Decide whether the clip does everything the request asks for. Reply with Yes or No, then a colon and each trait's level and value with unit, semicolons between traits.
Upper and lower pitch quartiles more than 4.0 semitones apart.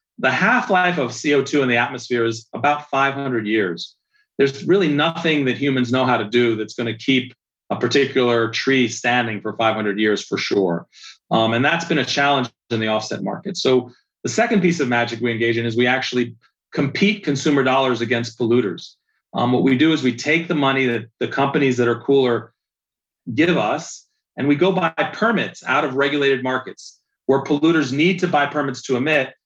No: average, 3.6 semitones